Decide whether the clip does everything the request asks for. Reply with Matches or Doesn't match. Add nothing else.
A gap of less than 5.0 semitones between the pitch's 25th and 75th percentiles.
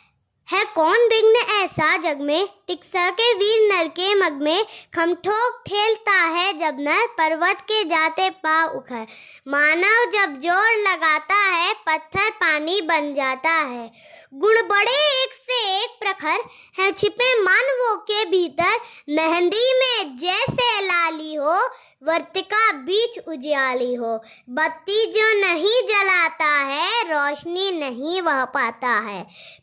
Doesn't match